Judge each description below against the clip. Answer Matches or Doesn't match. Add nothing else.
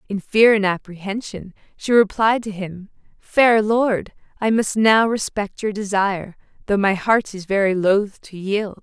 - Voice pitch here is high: Matches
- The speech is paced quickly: Doesn't match